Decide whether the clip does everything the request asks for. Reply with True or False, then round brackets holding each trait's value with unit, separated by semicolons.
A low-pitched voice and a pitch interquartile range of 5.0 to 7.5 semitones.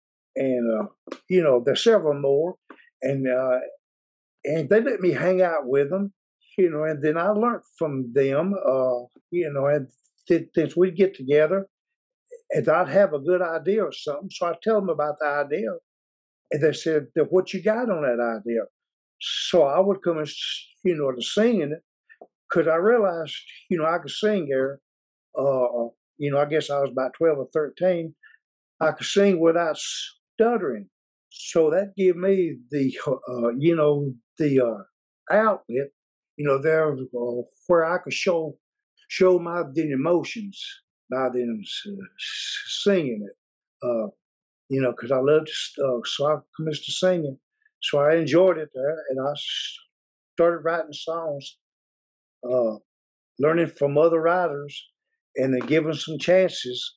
False (160 Hz; 5.5 semitones)